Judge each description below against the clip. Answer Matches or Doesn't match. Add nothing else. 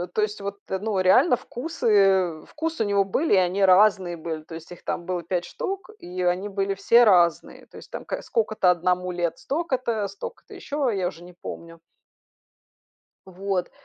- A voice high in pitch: Matches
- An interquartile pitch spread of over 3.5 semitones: Matches